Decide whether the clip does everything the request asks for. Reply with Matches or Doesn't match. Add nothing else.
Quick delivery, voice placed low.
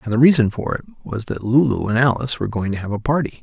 Matches